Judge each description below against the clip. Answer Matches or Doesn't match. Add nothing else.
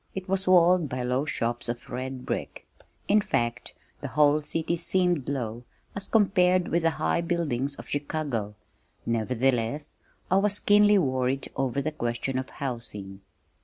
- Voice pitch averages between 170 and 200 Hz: Doesn't match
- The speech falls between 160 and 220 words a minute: Doesn't match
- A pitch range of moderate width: Doesn't match